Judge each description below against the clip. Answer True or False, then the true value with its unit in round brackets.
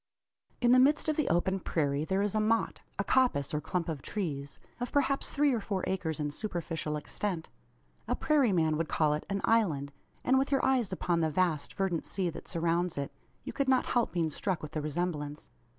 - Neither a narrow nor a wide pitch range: False (6.7 semitones)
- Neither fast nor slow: False (210 wpm)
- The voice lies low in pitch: False (180 Hz)